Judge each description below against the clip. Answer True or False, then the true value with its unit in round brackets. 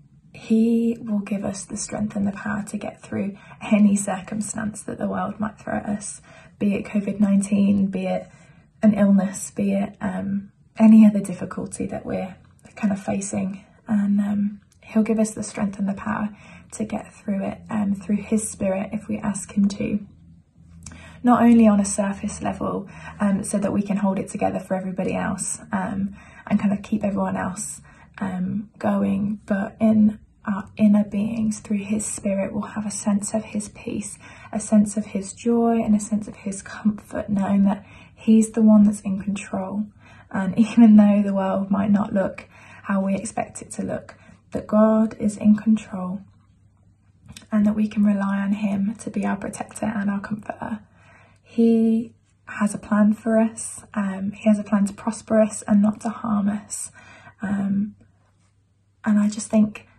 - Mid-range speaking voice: False (205 Hz)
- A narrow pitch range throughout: True (1.6 semitones)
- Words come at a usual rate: True (180 wpm)